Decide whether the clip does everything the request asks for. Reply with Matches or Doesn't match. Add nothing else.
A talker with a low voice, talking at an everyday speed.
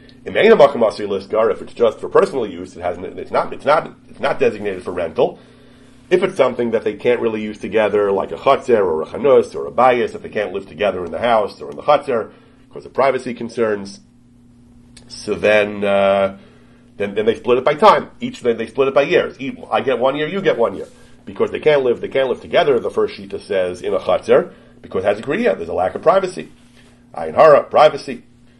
Doesn't match